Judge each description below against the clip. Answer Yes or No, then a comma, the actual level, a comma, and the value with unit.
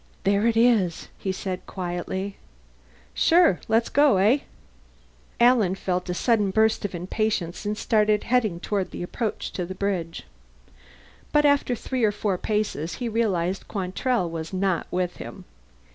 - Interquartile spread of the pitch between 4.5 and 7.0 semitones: No, average, 3.8 semitones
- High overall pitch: Yes, high, 200 Hz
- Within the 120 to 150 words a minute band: Yes, average, 145 wpm